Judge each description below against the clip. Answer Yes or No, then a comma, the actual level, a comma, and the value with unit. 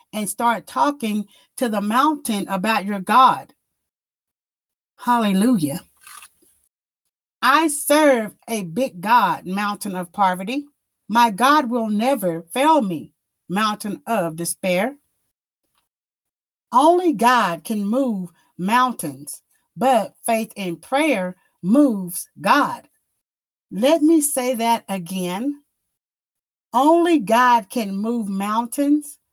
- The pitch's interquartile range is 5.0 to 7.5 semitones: Yes, wide, 5.6 semitones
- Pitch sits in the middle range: No, high, 230 Hz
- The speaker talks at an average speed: No, slow, 100 wpm